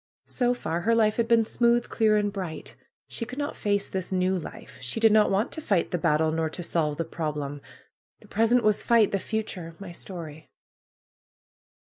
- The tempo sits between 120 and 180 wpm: No, average, 200 wpm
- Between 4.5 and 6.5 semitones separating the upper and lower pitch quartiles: Yes, average, 5.3 semitones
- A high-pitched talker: Yes, high, 200 Hz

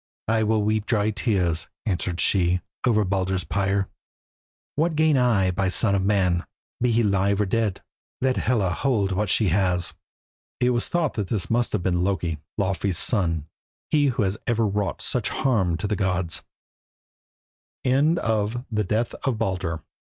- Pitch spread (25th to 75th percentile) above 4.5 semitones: No, average, 3.7 semitones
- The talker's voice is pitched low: Yes, low, 100 Hz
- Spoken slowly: No, average, 160 wpm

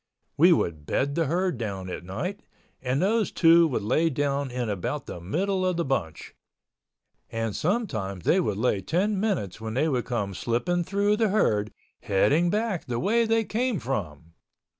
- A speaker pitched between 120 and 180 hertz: Yes, medium, 140 Hz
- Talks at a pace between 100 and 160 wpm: No, average, 170 wpm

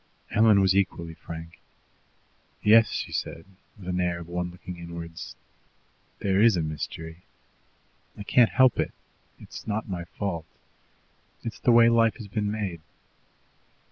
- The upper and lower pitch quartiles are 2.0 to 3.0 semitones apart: No, average, 4.2 semitones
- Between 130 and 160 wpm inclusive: Yes, average, 140 wpm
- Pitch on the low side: Yes, very low, 95 Hz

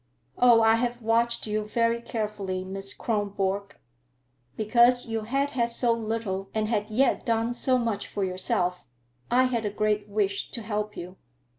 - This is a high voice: Yes, high, 220 Hz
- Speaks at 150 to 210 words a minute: Yes, average, 160 wpm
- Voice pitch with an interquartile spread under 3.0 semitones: Yes, narrow, 2.5 semitones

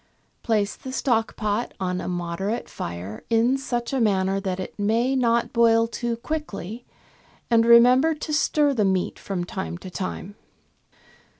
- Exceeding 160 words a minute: No, average, 155 wpm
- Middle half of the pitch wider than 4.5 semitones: No, average, 4.1 semitones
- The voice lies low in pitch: No, high, 225 Hz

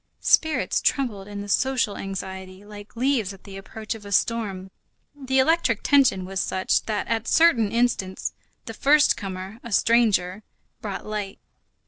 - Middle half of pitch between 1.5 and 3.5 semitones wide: No, average, 3.9 semitones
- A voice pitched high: Yes, high, 210 Hz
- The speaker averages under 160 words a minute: Yes, average, 150 wpm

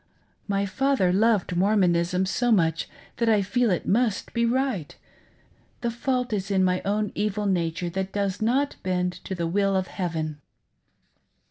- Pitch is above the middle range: Yes, high, 195 Hz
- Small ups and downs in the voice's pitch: No, average, 3.8 semitones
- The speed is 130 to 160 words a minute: Yes, average, 155 wpm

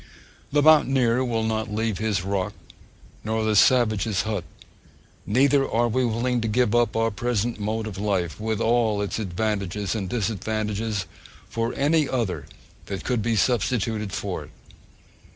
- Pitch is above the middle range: No, low, 110 Hz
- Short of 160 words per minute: Yes, average, 150 wpm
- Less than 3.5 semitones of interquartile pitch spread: Yes, average, 2.7 semitones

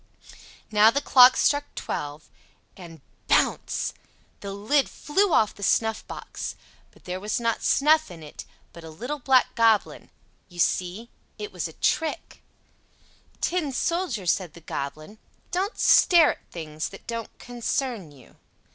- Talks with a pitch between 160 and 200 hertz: No, high, 225 Hz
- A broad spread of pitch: Yes, wide, 8.5 semitones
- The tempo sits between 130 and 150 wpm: Yes, slow, 135 wpm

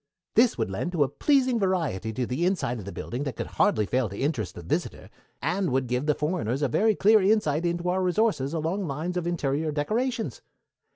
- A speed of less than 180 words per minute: No, fast, 205 wpm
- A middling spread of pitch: No, wide, 6.5 semitones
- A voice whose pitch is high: No, medium, 160 Hz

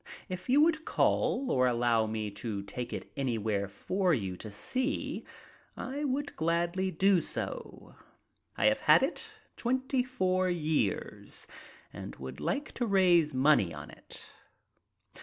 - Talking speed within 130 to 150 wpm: Yes, average, 140 wpm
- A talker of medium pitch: Yes, medium, 170 Hz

